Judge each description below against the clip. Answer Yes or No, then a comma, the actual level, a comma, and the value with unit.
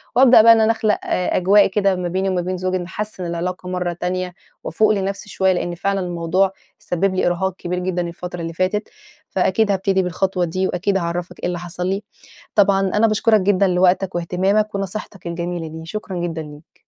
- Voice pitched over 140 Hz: Yes, medium, 185 Hz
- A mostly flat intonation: Yes, narrow, 2.0 semitones